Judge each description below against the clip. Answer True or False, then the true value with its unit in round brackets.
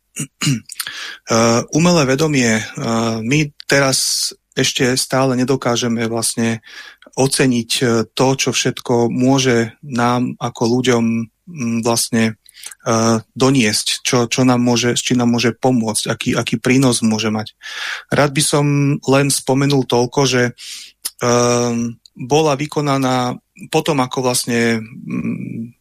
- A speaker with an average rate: False (100 wpm)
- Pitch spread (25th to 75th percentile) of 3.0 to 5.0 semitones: False (2.4 semitones)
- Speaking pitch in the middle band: False (125 Hz)